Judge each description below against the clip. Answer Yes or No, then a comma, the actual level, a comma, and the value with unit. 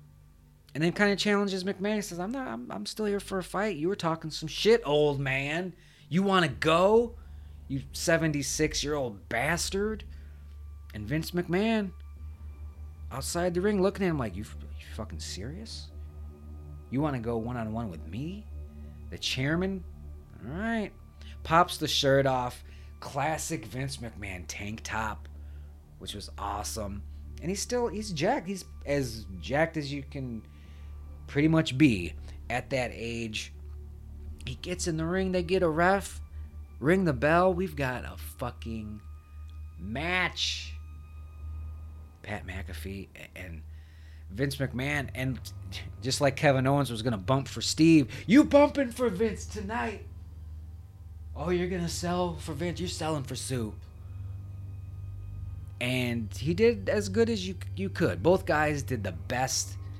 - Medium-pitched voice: No, low, 110 Hz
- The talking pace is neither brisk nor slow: Yes, average, 150 wpm